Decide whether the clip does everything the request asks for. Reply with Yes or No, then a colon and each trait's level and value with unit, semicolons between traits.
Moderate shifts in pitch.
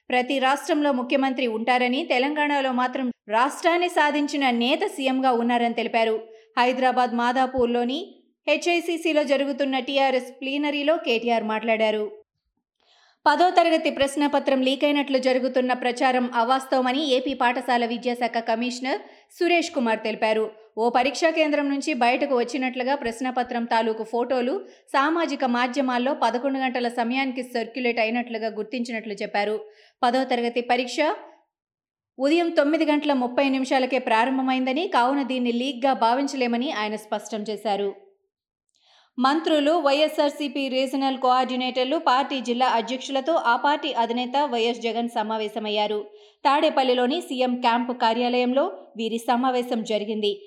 Yes: average, 3.0 semitones